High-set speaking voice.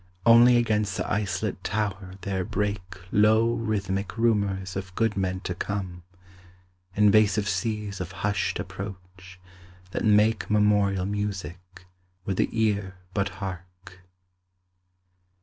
No: low, 100 Hz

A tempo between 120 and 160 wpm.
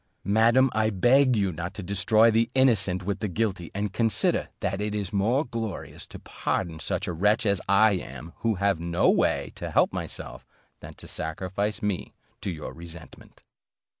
No: average, 175 wpm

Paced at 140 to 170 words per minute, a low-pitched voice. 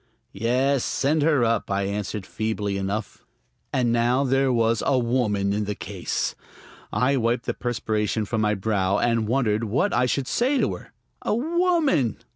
Yes: average, 165 wpm; low, 115 Hz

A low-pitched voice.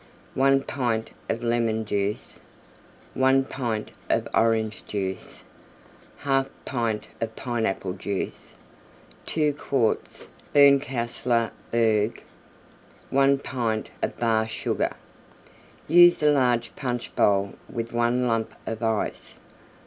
Yes: low, 115 Hz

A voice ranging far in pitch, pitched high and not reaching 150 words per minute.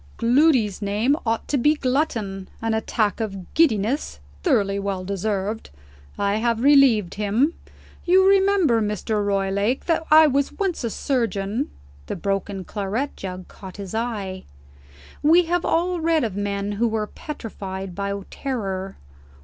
Yes: wide, 5.9 semitones; high, 220 Hz; average, 140 wpm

